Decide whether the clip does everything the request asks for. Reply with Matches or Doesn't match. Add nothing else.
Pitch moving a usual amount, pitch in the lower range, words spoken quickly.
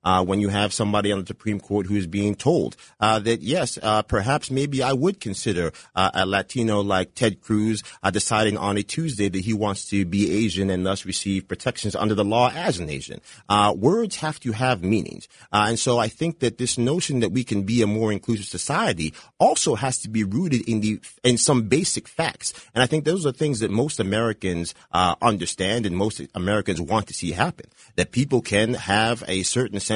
Matches